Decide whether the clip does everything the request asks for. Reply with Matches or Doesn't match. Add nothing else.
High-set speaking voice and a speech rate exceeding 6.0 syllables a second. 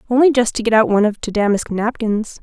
Matches